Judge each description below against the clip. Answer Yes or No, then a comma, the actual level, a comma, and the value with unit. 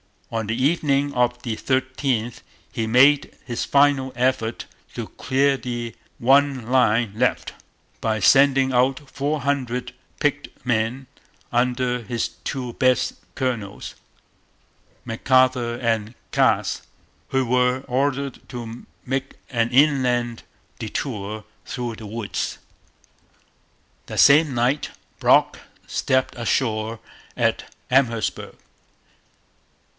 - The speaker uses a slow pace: Yes, slow, 100 wpm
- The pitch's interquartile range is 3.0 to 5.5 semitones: No, narrow, 2.5 semitones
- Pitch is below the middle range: Yes, low, 125 Hz